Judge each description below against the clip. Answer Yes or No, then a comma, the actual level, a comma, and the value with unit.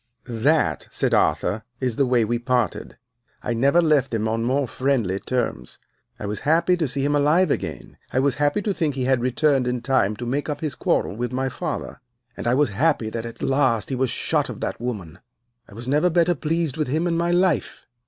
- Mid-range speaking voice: No, low, 130 Hz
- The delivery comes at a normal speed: No, fast, 215 wpm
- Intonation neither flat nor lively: Yes, average, 4.2 semitones